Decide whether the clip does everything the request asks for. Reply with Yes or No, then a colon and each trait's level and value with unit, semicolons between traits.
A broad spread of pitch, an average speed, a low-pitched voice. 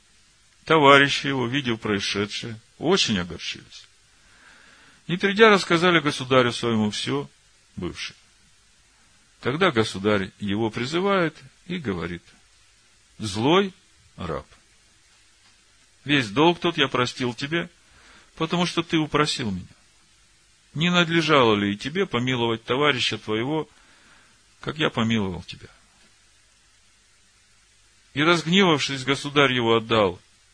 No: wide, 5.9 semitones; slow, 95 wpm; low, 115 Hz